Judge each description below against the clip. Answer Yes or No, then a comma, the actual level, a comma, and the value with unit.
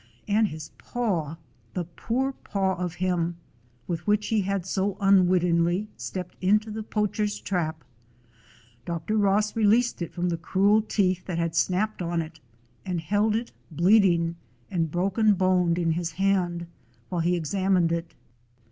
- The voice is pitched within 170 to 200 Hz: Yes, medium, 185 Hz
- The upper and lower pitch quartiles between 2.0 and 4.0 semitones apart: Yes, average, 3.3 semitones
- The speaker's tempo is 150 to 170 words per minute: Yes, average, 160 wpm